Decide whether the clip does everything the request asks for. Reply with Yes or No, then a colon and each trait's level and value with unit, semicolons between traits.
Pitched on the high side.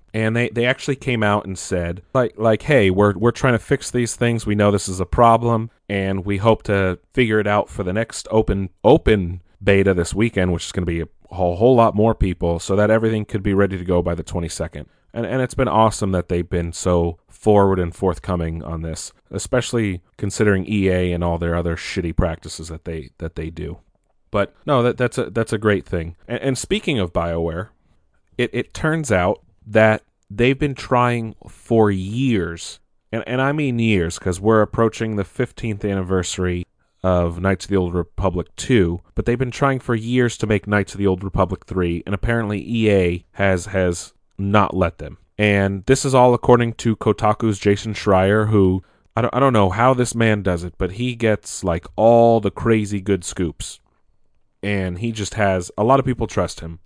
No: low, 100 Hz